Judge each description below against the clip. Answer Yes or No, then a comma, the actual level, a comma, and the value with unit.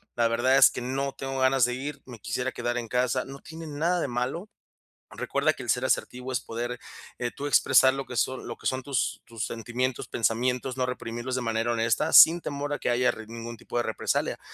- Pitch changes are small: Yes, narrow, 2.1 semitones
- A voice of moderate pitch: No, low, 125 Hz